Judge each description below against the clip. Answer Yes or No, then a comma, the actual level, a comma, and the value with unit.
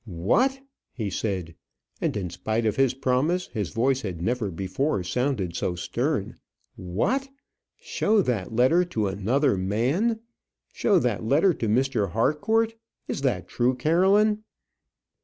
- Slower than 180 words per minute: Yes, slow, 135 wpm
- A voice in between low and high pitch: No, low, 125 Hz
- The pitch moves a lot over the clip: Yes, wide, 8.3 semitones